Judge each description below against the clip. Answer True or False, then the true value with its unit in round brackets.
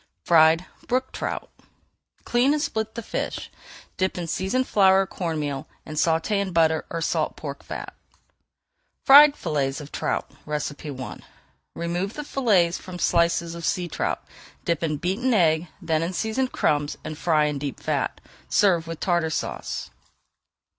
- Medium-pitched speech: True (170 Hz)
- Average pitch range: True (4.0 semitones)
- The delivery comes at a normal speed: True (155 wpm)